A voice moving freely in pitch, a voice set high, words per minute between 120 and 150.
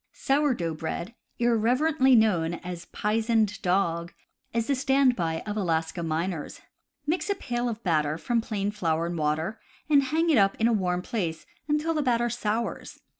No: wide, 6.4 semitones; high, 215 Hz; average, 170 wpm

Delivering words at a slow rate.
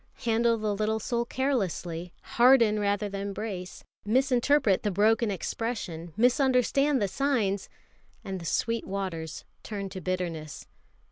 Yes: slow, 125 wpm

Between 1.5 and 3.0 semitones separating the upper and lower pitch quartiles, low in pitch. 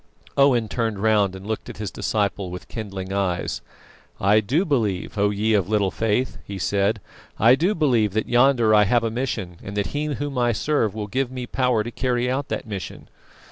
No: average, 3.9 semitones; low, 110 Hz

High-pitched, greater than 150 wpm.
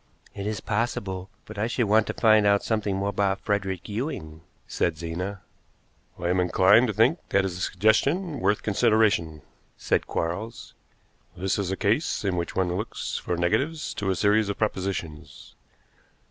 No: low, 100 Hz; average, 165 wpm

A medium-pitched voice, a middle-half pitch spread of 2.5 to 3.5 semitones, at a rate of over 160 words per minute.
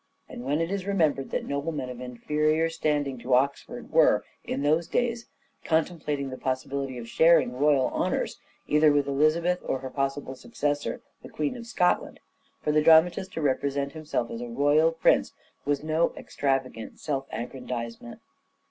No: medium, 145 Hz; average, 3.2 semitones; average, 155 wpm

